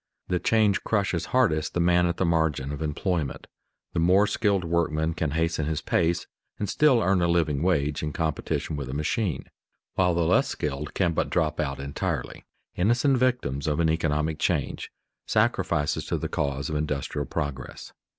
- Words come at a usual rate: Yes, average, 170 wpm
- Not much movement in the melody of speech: No, average, 3.3 semitones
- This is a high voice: No, very low, 80 Hz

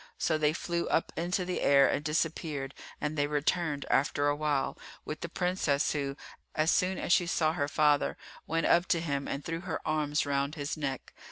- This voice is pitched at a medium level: Yes, medium, 155 Hz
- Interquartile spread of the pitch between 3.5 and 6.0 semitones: No, average, 2.7 semitones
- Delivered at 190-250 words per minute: Yes, average, 195 wpm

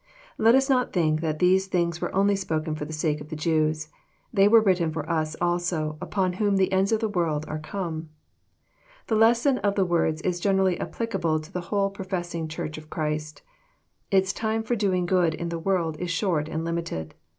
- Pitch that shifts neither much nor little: Yes, average, 3.7 semitones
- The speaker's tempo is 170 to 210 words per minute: Yes, average, 200 wpm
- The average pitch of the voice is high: No, medium, 175 Hz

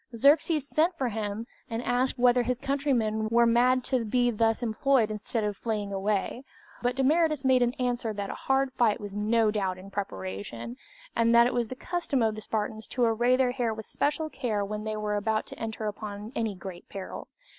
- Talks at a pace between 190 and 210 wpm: Yes, average, 200 wpm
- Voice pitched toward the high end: Yes, high, 230 Hz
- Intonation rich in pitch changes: No, average, 3.2 semitones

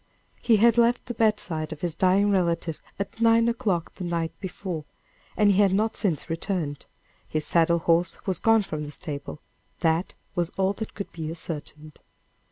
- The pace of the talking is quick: No, average, 175 wpm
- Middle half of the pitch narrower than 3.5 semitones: No, average, 4.2 semitones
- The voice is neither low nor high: Yes, medium, 180 Hz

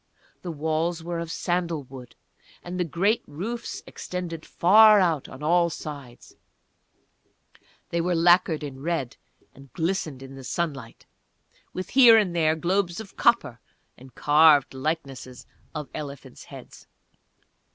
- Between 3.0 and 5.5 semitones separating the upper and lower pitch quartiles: Yes, average, 3.9 semitones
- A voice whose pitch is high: No, medium, 165 Hz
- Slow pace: Yes, slow, 130 wpm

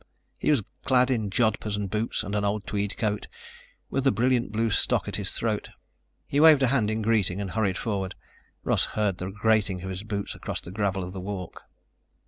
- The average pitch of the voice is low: Yes, low, 105 Hz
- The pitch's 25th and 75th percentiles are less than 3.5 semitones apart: Yes, average, 2.7 semitones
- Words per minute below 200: No, fast, 205 wpm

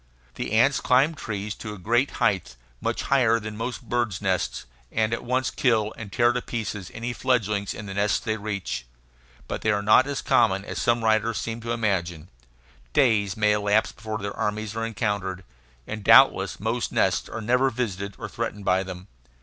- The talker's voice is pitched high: No, low, 110 Hz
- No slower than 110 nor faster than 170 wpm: No, average, 185 wpm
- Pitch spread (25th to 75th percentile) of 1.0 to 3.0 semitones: Yes, average, 2.7 semitones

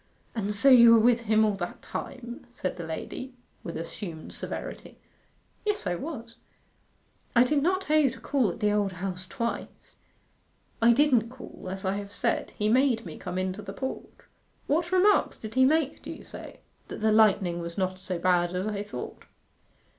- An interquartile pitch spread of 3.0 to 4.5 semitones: No, wide, 5.6 semitones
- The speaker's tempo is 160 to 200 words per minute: Yes, average, 185 wpm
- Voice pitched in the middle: No, high, 220 Hz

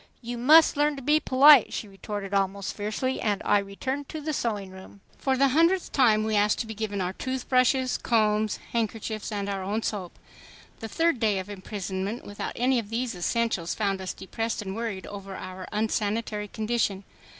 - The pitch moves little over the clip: No, average, 4.1 semitones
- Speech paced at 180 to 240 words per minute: Yes, average, 185 wpm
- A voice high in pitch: Yes, high, 215 Hz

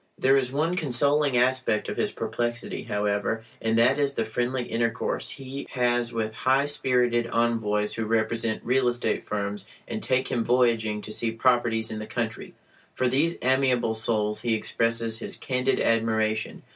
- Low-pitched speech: Yes, low, 120 Hz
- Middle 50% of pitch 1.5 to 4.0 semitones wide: Yes, narrow, 2.5 semitones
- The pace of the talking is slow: No, average, 160 wpm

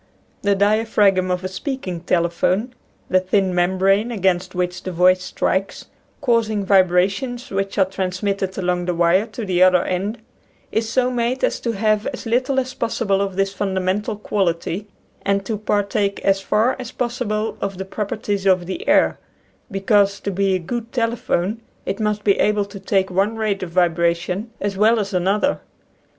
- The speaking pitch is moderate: No, high, 195 Hz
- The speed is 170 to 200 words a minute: Yes, average, 175 wpm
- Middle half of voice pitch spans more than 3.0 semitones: No, average, 2.7 semitones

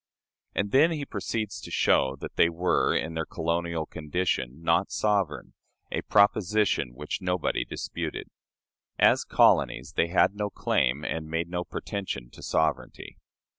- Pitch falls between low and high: No, very low, 85 Hz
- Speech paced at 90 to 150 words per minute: Yes, average, 140 wpm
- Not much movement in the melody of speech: No, average, 4.2 semitones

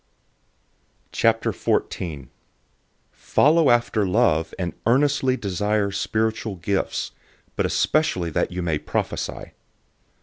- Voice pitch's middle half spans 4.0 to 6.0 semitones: Yes, wide, 5.4 semitones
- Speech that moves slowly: Yes, slow, 90 wpm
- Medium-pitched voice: No, low, 105 Hz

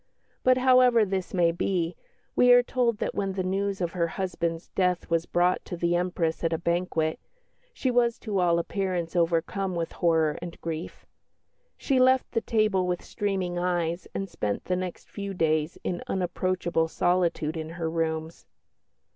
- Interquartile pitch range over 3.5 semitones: No, average, 2.8 semitones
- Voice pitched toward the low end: No, medium, 180 Hz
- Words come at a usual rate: Yes, average, 165 wpm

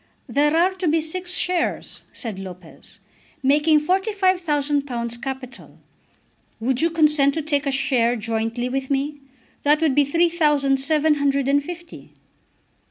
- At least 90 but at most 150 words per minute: Yes, average, 140 wpm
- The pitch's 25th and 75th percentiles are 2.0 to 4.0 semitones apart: Yes, average, 3.5 semitones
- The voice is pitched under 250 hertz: No, very high, 285 Hz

